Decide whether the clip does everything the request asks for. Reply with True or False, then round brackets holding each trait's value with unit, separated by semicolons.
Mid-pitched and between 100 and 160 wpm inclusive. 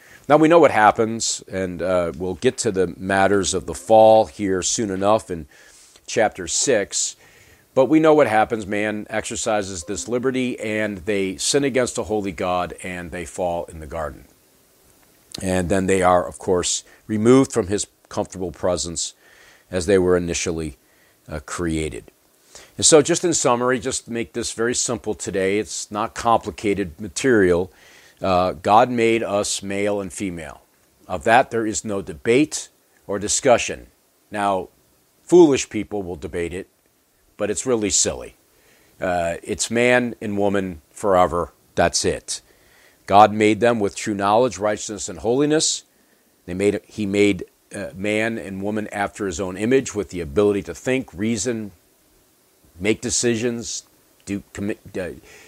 False (105 Hz; 150 wpm)